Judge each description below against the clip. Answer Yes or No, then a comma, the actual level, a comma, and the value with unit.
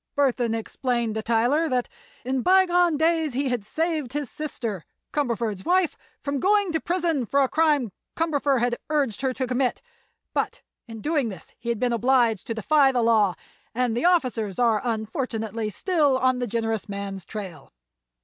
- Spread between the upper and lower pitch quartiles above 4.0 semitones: Yes, average, 4.8 semitones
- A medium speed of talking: Yes, average, 170 wpm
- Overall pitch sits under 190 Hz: No, very high, 250 Hz